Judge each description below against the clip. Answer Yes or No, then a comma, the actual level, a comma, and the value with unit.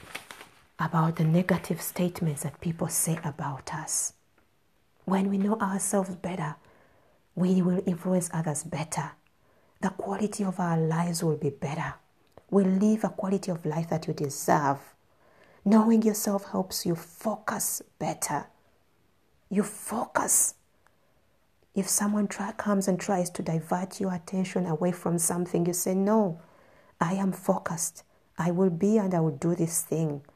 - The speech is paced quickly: No, average, 140 wpm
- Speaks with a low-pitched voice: No, medium, 180 Hz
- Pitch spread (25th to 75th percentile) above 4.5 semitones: No, average, 3.2 semitones